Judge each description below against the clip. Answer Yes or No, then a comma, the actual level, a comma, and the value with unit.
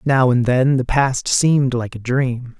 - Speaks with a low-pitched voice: Yes, low, 130 Hz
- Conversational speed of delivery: No, fast, 210 wpm